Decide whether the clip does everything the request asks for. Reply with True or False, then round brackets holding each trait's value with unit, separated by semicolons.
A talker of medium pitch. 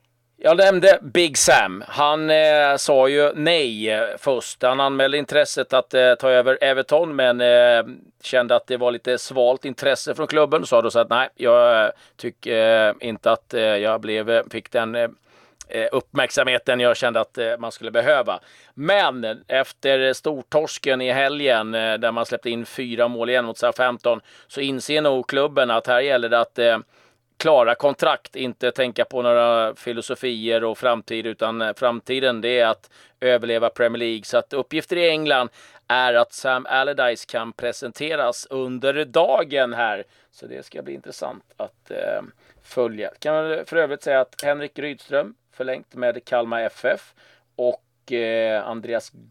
False (125 Hz)